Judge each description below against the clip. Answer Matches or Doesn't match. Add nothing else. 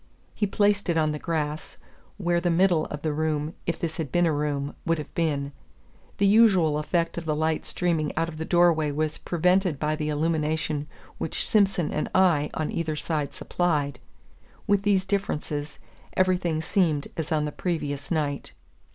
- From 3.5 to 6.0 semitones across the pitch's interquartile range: Doesn't match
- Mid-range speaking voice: Matches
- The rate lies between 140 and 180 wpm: Matches